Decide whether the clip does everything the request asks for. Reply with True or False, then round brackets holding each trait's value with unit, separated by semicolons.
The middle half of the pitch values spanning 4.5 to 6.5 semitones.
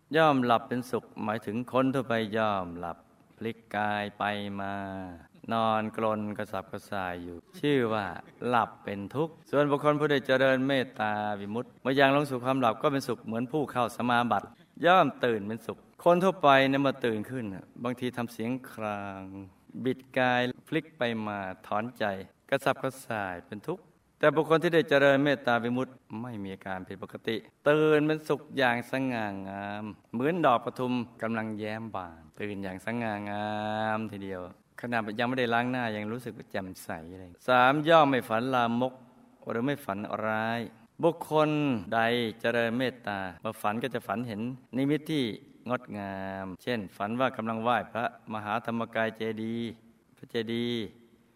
False (3.8 semitones)